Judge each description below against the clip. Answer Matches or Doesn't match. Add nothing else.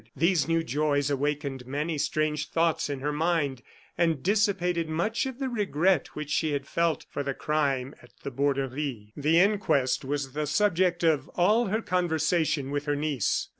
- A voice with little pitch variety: Doesn't match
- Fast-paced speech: Doesn't match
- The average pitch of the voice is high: Doesn't match